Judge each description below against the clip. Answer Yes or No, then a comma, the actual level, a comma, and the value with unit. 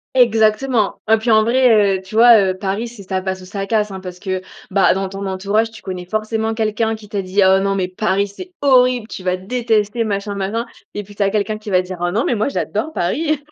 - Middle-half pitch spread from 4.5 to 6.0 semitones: No, average, 2.7 semitones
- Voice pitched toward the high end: Yes, high, 210 Hz